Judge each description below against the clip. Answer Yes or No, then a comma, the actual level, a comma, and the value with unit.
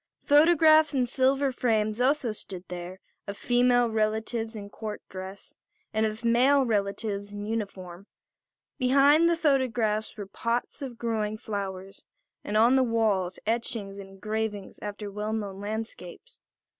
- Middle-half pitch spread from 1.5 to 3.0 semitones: No, average, 3.4 semitones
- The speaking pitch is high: Yes, high, 220 Hz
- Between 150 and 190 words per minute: No, slow, 135 wpm